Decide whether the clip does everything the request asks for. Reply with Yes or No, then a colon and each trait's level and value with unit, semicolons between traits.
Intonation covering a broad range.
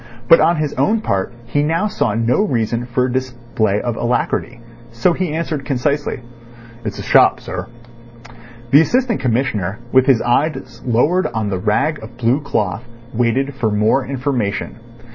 No: average, 4.2 semitones